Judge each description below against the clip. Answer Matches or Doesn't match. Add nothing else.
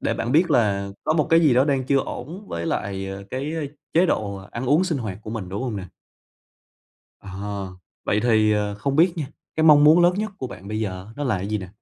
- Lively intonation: Matches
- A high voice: Doesn't match